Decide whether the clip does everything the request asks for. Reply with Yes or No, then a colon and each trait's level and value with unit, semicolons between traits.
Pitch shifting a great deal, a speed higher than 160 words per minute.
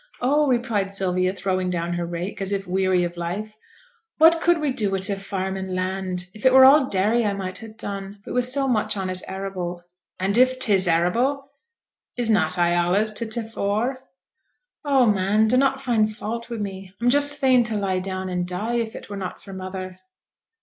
No: average, 4.3 semitones; average, 200 wpm